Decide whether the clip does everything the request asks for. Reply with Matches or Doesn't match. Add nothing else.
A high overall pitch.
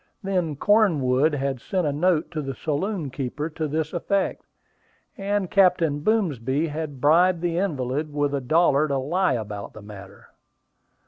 Doesn't match